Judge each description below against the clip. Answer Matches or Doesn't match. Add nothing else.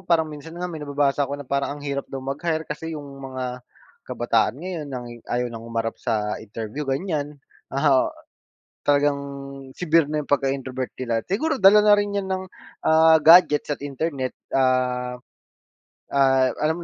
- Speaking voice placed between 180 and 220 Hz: Doesn't match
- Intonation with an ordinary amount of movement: Matches